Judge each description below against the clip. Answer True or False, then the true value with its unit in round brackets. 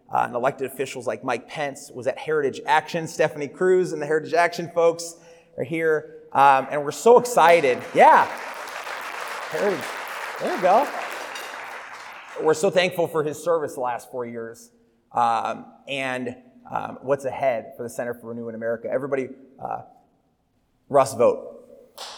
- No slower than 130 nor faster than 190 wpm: True (155 wpm)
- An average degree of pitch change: True (4.8 semitones)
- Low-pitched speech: False (155 Hz)